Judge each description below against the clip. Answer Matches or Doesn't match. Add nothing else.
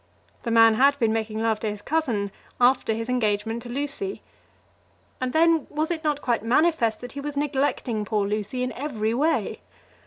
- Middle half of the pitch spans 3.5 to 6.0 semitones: Matches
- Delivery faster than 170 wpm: Matches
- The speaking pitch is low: Doesn't match